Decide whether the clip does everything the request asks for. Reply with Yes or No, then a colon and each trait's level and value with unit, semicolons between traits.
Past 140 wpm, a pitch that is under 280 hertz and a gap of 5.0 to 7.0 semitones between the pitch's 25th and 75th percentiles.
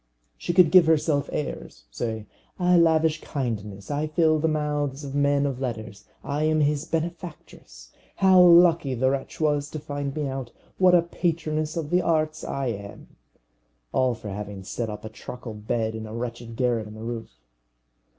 Yes: average, 175 wpm; medium, 140 Hz; wide, 5.5 semitones